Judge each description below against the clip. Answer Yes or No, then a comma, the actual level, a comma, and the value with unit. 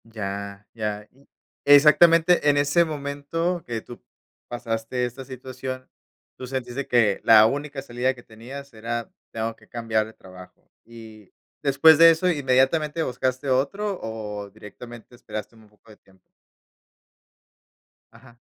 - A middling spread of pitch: Yes, average, 4.2 semitones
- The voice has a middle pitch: No, low, 125 Hz